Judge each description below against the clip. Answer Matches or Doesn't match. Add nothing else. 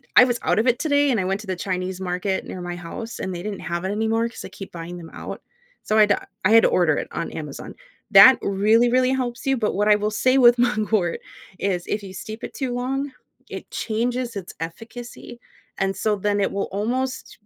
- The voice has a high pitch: Matches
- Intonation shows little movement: Doesn't match